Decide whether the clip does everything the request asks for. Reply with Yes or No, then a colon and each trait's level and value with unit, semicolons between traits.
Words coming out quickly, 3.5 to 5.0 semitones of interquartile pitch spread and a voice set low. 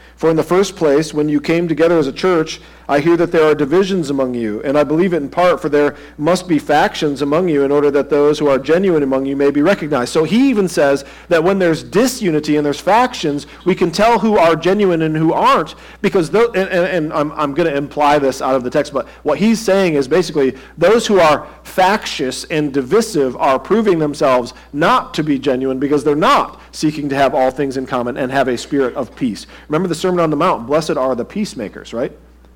No: fast, 230 wpm; average, 4.1 semitones; medium, 155 Hz